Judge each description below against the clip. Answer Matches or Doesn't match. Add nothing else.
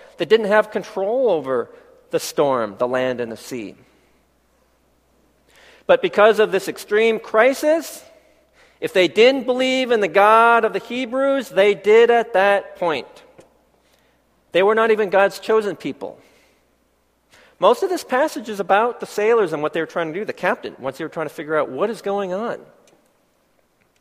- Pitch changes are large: Matches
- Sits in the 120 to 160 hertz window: Doesn't match